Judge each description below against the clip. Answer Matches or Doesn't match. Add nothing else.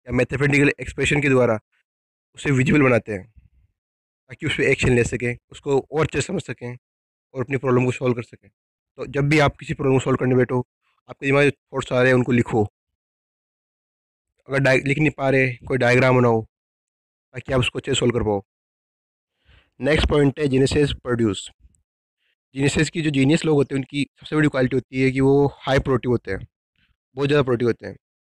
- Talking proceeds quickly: Matches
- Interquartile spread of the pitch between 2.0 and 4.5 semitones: Matches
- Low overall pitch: Matches